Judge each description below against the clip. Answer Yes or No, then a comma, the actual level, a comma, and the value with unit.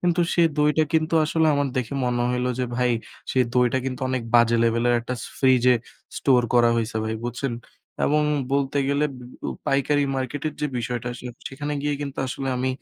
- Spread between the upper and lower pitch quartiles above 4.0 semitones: No, average, 2.8 semitones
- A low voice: Yes, low, 130 Hz